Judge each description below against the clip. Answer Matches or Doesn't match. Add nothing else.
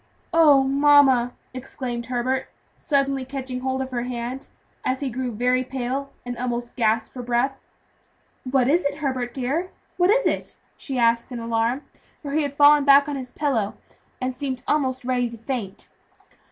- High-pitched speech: Matches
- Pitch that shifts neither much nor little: Doesn't match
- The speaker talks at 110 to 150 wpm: Doesn't match